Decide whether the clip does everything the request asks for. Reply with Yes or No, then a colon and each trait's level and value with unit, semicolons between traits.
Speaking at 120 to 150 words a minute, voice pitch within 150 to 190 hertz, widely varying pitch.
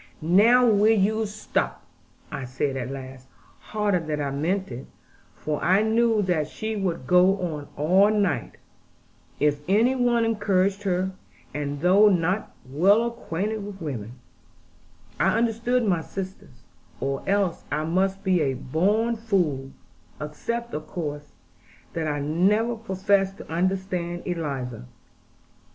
Yes: slow, 135 wpm; medium, 185 Hz; wide, 5.8 semitones